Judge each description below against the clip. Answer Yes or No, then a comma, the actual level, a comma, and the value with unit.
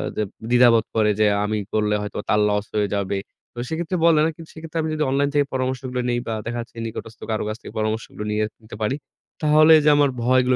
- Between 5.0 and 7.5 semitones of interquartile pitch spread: Yes, average, 5.3 semitones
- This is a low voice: Yes, low, 125 Hz